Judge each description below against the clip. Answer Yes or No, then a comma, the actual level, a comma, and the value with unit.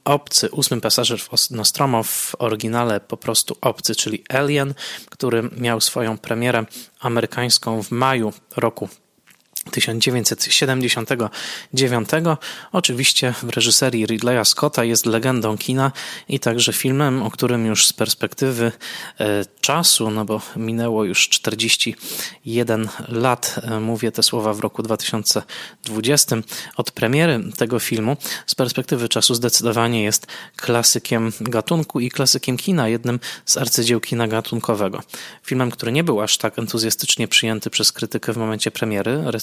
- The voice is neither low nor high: No, low, 115 Hz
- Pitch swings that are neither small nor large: No, narrow, 2.3 semitones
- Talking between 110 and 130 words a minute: Yes, average, 125 wpm